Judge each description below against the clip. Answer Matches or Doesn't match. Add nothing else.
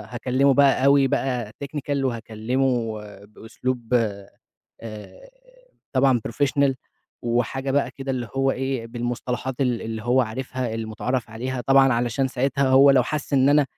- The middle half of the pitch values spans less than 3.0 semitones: Matches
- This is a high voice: Doesn't match